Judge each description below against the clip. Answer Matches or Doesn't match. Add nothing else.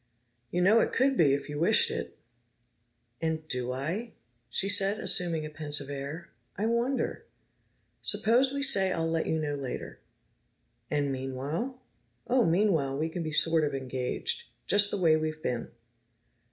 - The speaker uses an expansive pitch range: Matches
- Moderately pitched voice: Matches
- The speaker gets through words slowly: Doesn't match